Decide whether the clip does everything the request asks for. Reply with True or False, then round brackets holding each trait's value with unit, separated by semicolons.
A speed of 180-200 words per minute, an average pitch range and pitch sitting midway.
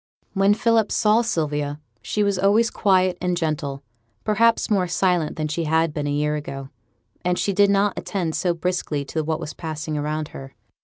True (185 wpm; 4.7 semitones; 170 Hz)